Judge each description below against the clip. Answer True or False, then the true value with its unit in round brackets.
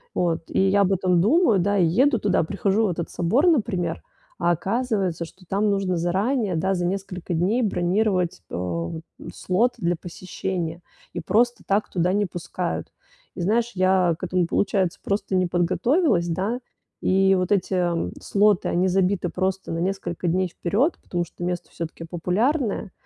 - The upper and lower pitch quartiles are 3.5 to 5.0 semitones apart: False (2.8 semitones)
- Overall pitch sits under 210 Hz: True (185 Hz)